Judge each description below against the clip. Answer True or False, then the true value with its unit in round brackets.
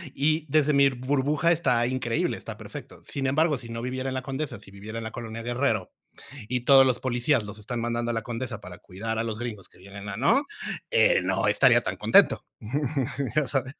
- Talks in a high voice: False (125 Hz)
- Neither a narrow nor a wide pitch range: True (3.5 semitones)